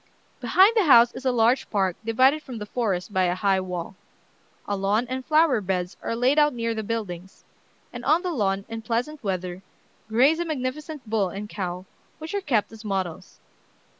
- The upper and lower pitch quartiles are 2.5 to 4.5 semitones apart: No, wide, 5.5 semitones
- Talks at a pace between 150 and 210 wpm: Yes, average, 190 wpm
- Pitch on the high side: Yes, high, 225 Hz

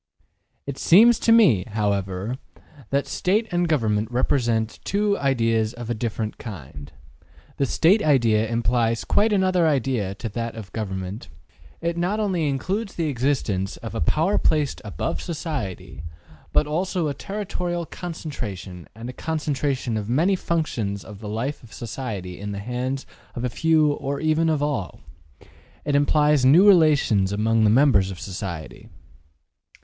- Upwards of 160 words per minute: No, average, 150 wpm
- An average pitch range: No, wide, 6.9 semitones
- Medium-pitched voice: No, low, 130 Hz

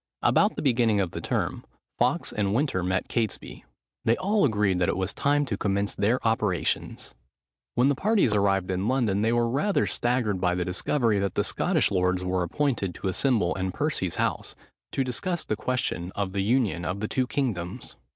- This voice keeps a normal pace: Yes, average, 190 wpm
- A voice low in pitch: Yes, low, 105 Hz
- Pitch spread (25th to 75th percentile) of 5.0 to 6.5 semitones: Yes, average, 5.3 semitones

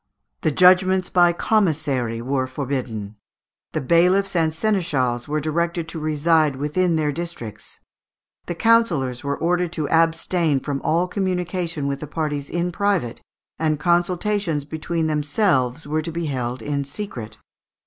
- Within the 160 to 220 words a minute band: No, average, 140 wpm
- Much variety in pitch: No, average, 3.9 semitones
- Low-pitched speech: No, medium, 160 Hz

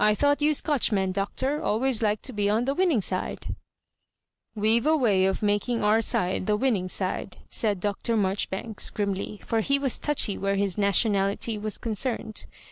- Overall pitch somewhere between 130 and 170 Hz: No, high, 215 Hz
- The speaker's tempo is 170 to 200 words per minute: Yes, average, 180 wpm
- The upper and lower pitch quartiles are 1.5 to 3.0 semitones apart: No, average, 3.5 semitones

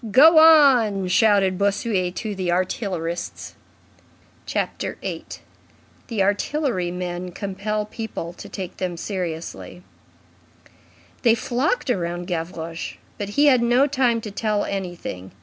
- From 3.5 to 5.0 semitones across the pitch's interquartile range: Yes, average, 4.7 semitones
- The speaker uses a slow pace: Yes, slow, 115 wpm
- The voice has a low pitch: No, high, 200 Hz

